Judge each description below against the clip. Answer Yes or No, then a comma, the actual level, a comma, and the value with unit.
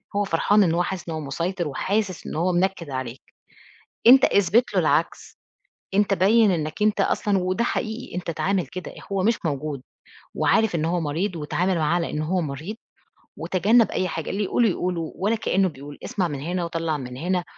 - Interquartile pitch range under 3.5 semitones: No, average, 3.8 semitones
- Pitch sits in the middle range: Yes, medium, 180 Hz